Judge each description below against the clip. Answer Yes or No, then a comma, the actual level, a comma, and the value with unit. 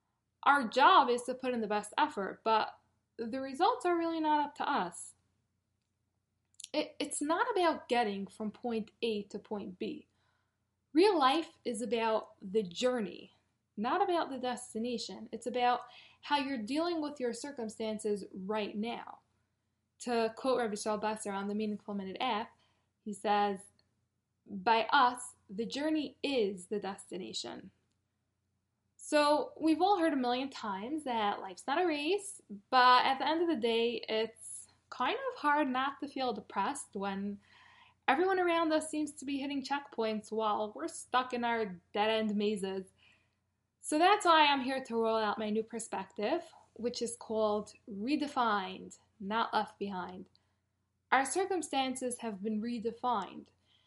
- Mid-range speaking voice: No, high, 230 Hz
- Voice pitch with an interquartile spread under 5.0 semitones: No, wide, 5.5 semitones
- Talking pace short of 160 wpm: Yes, average, 150 wpm